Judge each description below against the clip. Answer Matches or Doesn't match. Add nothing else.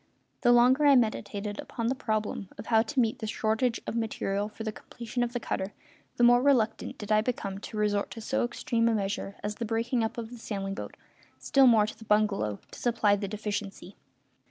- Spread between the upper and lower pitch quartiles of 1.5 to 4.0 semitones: Matches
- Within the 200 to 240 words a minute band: Matches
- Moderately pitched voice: Doesn't match